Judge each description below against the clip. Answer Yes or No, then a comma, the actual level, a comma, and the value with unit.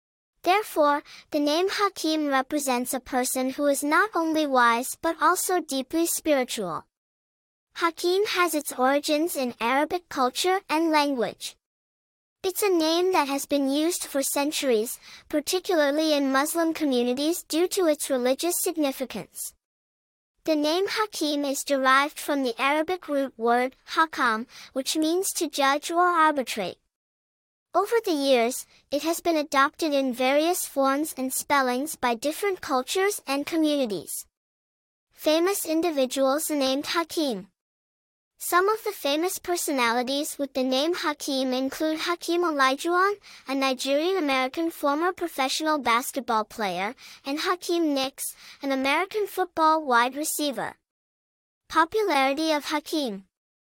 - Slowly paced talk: Yes, slow, 125 wpm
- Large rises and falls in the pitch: No, average, 4.1 semitones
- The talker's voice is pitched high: Yes, very high, 295 Hz